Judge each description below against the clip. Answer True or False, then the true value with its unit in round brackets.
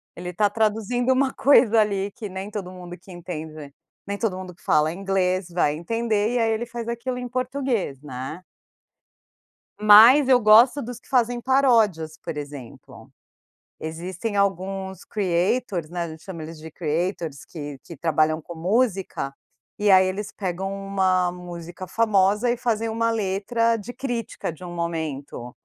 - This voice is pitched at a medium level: False (195 Hz)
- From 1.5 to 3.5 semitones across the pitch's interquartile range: False (5.1 semitones)